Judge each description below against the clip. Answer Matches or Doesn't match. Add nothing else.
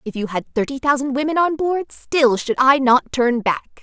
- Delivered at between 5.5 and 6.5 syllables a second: Doesn't match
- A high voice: Matches